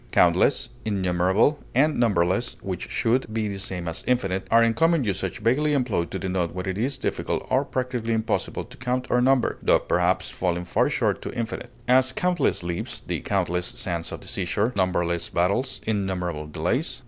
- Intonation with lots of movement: Yes, wide, 5.8 semitones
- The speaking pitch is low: Yes, low, 105 Hz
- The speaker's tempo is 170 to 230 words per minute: Yes, average, 175 wpm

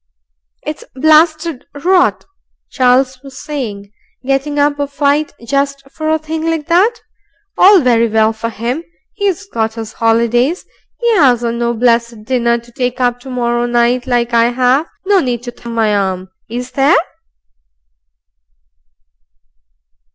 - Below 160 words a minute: Yes, average, 140 wpm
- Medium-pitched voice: No, very high, 250 Hz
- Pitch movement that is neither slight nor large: Yes, average, 3.9 semitones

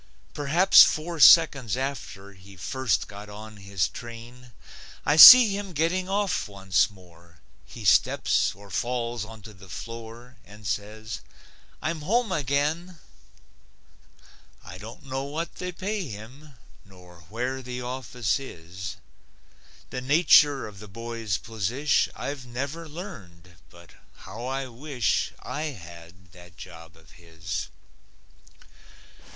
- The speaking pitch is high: No, low, 120 Hz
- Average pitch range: No, wide, 6.9 semitones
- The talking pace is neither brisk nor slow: No, slow, 125 wpm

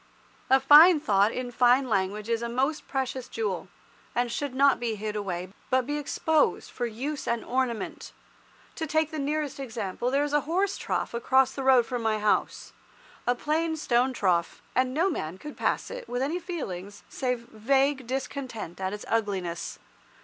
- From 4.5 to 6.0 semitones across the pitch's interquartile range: Yes, average, 4.8 semitones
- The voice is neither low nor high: No, very high, 255 Hz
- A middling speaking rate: Yes, average, 175 wpm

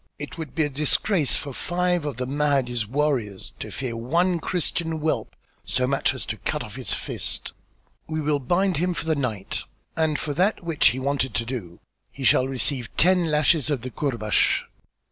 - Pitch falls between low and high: Yes, medium, 145 Hz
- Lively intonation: No, average, 4.1 semitones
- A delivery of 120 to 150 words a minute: No, average, 185 wpm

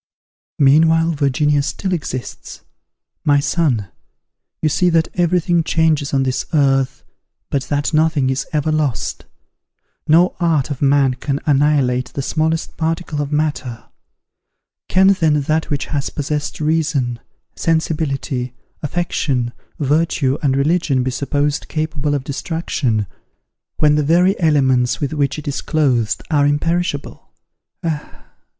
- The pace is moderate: No, slow, 130 wpm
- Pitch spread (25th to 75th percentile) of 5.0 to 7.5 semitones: No, average, 2.9 semitones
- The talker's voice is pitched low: No, medium, 150 Hz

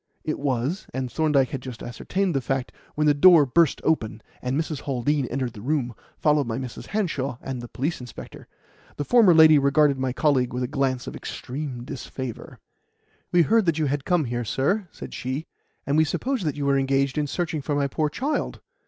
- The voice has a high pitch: No, medium, 140 Hz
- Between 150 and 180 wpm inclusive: No, average, 195 wpm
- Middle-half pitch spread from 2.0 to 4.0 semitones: Yes, average, 3.4 semitones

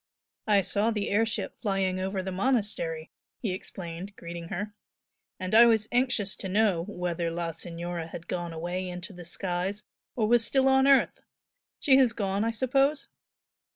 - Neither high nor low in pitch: No, high, 195 Hz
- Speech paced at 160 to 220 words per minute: Yes, average, 165 wpm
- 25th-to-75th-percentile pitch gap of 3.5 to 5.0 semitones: Yes, average, 4.4 semitones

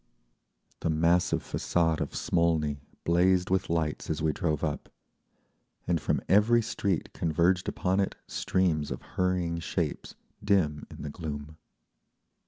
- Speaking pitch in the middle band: No, very low, 85 Hz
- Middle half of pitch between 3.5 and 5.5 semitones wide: No, average, 3.0 semitones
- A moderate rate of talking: No, slow, 130 wpm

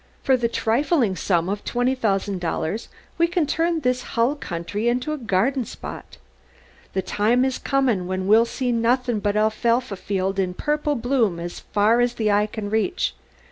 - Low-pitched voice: No, high, 230 Hz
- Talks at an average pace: Yes, average, 175 wpm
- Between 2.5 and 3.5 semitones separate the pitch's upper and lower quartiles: No, average, 4.2 semitones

